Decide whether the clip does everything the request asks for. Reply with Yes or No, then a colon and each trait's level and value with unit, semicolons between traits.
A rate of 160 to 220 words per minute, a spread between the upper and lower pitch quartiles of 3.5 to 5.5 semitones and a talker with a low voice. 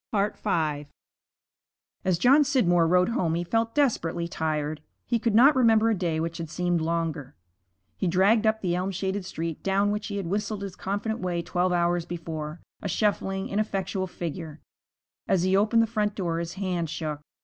No: average, 175 wpm; average, 3.9 semitones; medium, 185 Hz